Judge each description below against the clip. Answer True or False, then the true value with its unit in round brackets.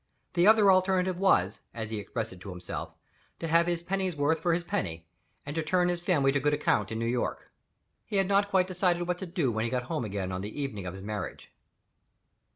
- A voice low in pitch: False (150 Hz)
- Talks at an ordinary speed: False (220 wpm)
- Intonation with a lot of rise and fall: True (8.8 semitones)